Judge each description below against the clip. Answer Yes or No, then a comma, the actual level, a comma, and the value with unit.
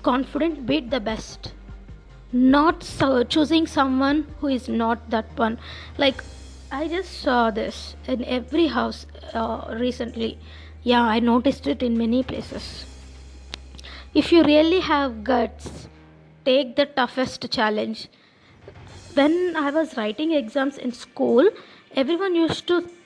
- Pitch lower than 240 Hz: No, very high, 260 Hz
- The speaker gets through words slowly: Yes, slow, 125 wpm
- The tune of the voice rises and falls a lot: No, average, 4.7 semitones